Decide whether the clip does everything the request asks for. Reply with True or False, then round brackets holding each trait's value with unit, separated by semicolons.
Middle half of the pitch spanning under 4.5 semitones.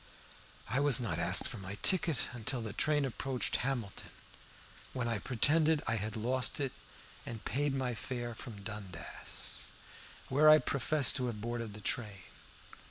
True (3.9 semitones)